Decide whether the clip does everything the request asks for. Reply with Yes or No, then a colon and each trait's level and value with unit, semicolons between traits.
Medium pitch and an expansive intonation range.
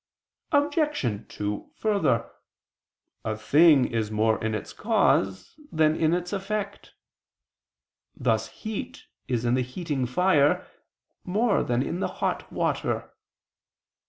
Yes: medium, 150 Hz; wide, 9.0 semitones